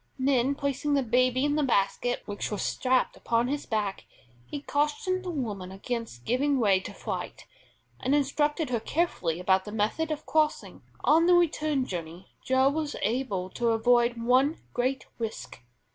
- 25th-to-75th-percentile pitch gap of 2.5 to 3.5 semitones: No, average, 5.0 semitones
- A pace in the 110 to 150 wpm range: No, average, 160 wpm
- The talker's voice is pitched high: Yes, very high, 255 Hz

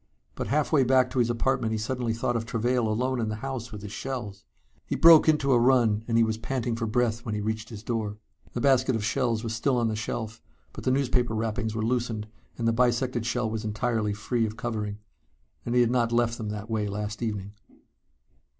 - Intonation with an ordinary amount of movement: No, narrow, 2.2 semitones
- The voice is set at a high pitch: No, low, 115 Hz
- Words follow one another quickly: Yes, fast, 220 wpm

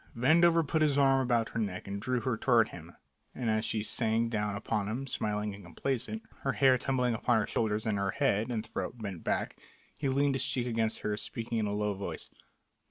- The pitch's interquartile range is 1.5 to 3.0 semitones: No, average, 3.9 semitones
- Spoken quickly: Yes, fast, 215 wpm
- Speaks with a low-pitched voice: Yes, low, 115 Hz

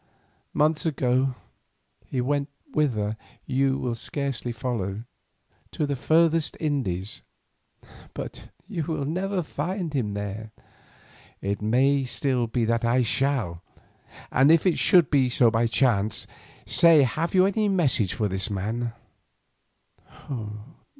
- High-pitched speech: No, low, 130 Hz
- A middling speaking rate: No, slow, 115 wpm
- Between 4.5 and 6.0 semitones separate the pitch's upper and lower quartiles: Yes, average, 5.3 semitones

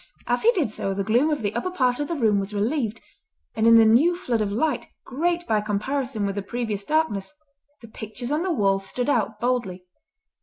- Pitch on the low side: No, high, 230 Hz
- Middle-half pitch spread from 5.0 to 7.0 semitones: Yes, wide, 5.6 semitones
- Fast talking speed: Yes, fast, 215 wpm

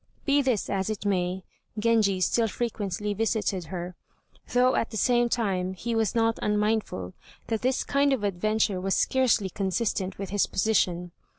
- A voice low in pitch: No, high, 210 Hz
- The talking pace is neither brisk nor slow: Yes, average, 160 wpm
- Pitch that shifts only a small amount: No, average, 3.4 semitones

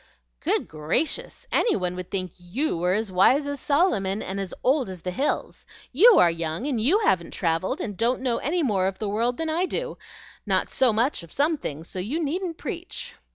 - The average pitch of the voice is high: Yes, high, 220 Hz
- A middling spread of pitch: No, wide, 8.0 semitones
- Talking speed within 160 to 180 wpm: No, fast, 205 wpm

